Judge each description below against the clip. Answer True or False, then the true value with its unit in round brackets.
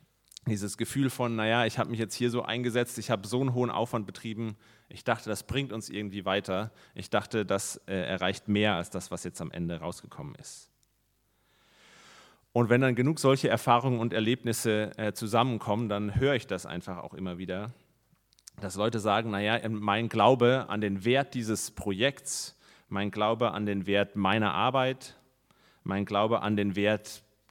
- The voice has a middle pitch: False (110 Hz)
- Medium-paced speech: True (175 wpm)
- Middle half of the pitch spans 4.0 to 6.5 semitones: False (2.9 semitones)